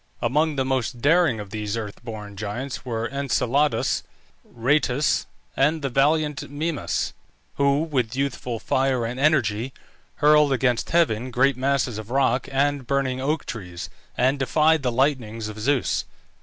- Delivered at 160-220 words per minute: No, average, 140 wpm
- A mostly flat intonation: No, average, 3.6 semitones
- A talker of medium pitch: No, low, 130 Hz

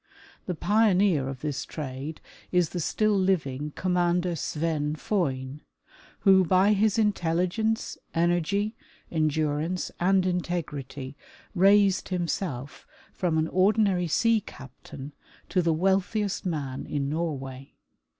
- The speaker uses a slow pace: Yes, slow, 110 wpm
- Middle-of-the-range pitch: Yes, medium, 175 Hz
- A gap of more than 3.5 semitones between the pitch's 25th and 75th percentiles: Yes, average, 4.5 semitones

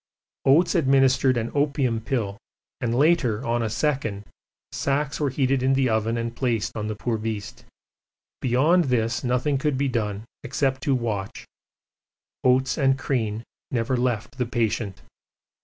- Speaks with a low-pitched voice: Yes, low, 125 Hz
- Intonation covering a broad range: No, average, 3.2 semitones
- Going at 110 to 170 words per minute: Yes, average, 145 wpm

